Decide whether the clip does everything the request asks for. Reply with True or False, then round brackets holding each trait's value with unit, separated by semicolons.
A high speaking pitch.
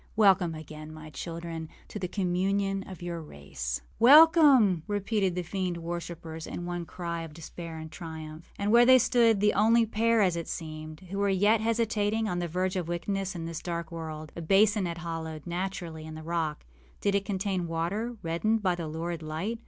False (175 Hz)